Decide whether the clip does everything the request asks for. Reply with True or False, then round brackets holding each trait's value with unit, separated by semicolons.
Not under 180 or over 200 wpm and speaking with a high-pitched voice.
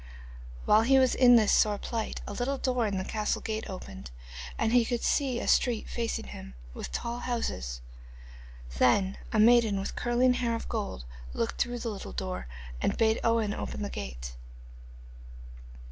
False (170 wpm; 225 Hz)